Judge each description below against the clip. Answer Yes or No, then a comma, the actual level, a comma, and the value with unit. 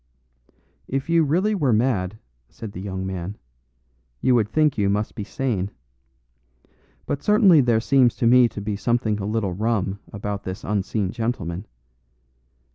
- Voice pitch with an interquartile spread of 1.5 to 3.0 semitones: No, average, 4.3 semitones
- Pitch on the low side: Yes, low, 110 Hz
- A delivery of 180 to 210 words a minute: No, average, 150 wpm